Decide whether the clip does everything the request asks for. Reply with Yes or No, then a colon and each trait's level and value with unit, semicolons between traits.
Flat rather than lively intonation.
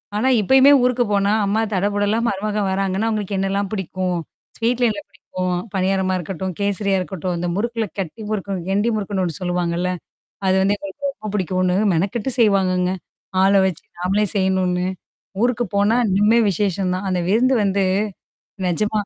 Yes: narrow, 2.3 semitones